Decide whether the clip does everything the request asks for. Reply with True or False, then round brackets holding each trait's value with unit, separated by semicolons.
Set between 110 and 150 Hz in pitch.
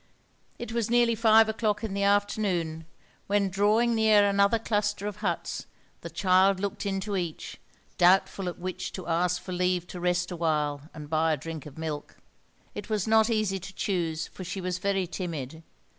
False (190 Hz)